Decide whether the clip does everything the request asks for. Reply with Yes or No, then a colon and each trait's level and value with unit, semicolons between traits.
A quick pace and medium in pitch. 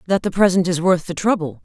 Yes: fast, 255 wpm; medium, 180 Hz